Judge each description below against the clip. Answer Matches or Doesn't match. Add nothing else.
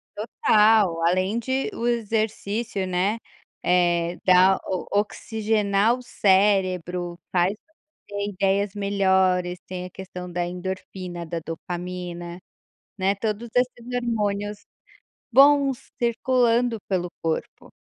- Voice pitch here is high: Matches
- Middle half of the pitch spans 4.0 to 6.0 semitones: Doesn't match